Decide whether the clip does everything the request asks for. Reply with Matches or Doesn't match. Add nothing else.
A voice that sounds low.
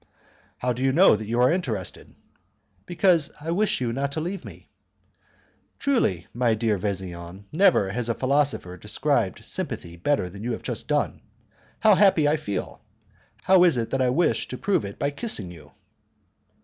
Matches